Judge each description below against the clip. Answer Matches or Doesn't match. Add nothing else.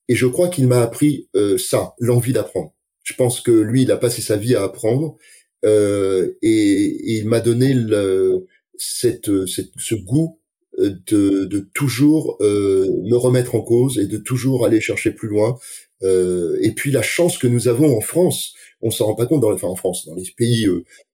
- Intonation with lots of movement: Matches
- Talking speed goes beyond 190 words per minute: Matches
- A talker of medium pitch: Doesn't match